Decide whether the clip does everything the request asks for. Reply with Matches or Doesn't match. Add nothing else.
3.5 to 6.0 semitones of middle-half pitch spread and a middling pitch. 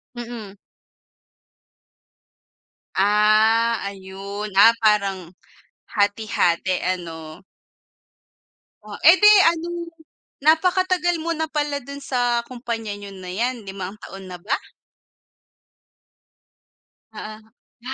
Doesn't match